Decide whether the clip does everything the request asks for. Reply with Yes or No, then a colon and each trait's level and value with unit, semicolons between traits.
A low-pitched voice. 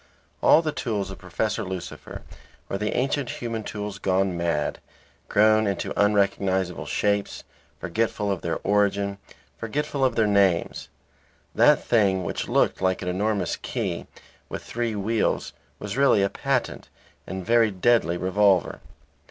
Yes: low, 100 Hz